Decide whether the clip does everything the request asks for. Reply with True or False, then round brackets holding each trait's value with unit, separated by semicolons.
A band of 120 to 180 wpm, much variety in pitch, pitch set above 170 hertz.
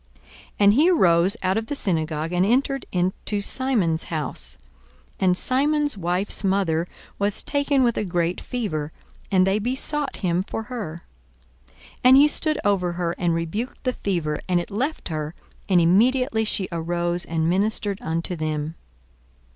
True (155 wpm; 5.9 semitones; 190 Hz)